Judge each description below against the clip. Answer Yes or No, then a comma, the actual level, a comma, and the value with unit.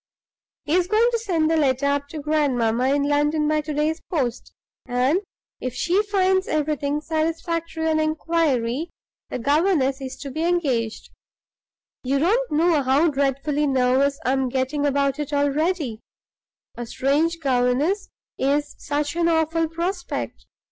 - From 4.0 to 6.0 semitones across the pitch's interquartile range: No, average, 3.4 semitones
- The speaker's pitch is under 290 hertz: No, very high, 295 Hz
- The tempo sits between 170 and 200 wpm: No, average, 145 wpm